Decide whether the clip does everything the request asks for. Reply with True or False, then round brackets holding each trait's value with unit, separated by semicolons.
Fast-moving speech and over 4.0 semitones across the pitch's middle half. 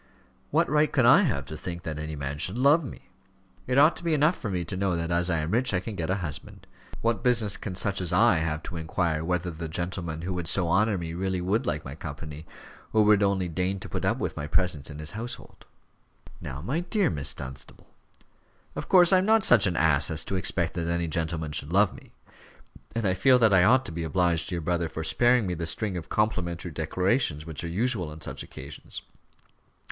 True (235 wpm; 4.9 semitones)